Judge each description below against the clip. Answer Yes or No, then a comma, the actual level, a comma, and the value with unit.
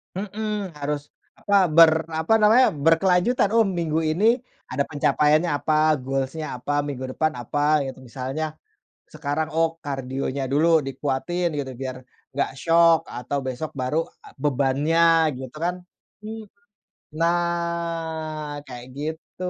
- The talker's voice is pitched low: No, medium, 155 Hz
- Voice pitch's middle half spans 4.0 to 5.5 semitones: No, average, 3.2 semitones